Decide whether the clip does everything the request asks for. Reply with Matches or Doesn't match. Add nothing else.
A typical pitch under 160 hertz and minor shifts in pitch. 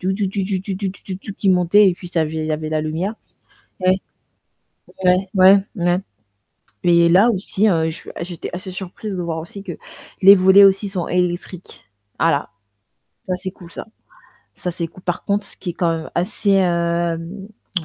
Doesn't match